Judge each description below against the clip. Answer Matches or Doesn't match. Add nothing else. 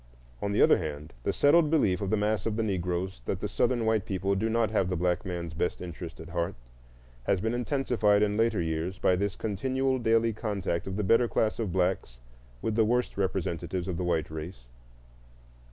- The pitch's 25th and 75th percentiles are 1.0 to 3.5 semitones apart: Doesn't match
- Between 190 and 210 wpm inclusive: Matches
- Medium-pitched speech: Doesn't match